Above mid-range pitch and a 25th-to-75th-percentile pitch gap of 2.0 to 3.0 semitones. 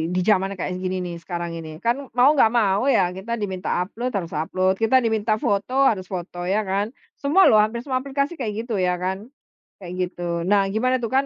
No: high, 205 Hz; average, 4.3 semitones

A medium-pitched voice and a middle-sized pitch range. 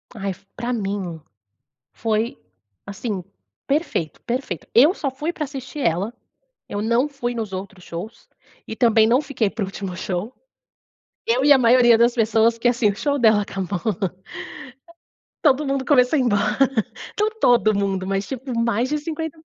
No: high, 230 Hz; average, 4.6 semitones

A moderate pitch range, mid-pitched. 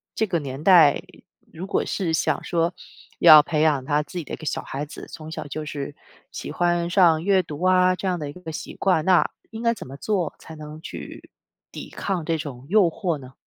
Yes: average, 3.4 semitones; medium, 165 Hz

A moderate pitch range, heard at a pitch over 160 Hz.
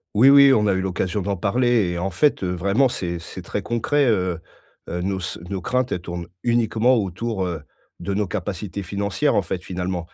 No: average, 4.5 semitones; low, 100 Hz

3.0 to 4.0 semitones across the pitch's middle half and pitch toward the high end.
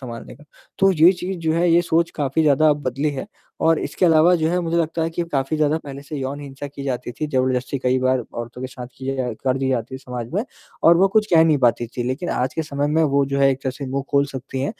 No: average, 3.6 semitones; medium, 140 Hz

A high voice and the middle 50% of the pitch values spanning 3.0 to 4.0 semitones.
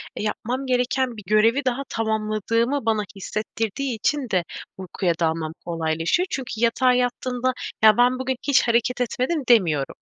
Yes: high, 235 Hz; average, 3.4 semitones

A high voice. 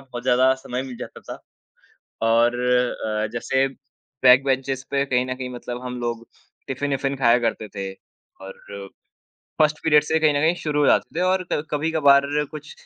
No: low, 130 Hz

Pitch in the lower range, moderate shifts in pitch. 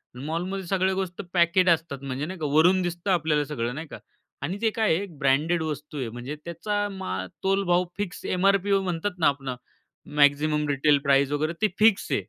No: medium, 165 Hz; average, 4.7 semitones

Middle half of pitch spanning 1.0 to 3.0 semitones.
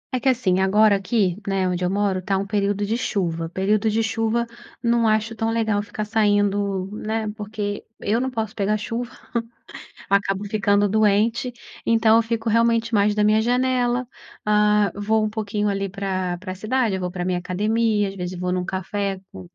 Yes: narrow, 2.4 semitones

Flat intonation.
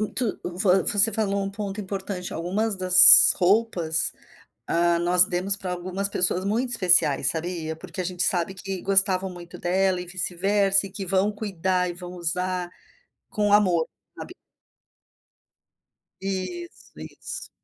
Yes: narrow, 1.9 semitones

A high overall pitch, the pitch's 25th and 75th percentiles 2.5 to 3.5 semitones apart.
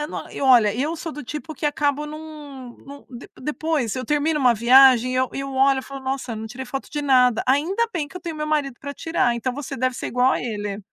Yes: very high, 270 Hz; average, 3.1 semitones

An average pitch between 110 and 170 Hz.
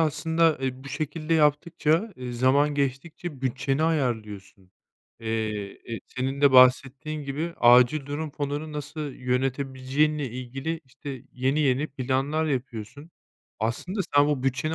Yes: medium, 140 Hz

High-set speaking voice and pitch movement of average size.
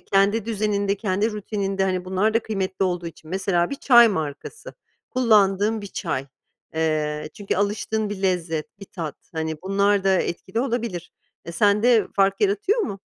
Yes: high, 195 Hz; average, 3.0 semitones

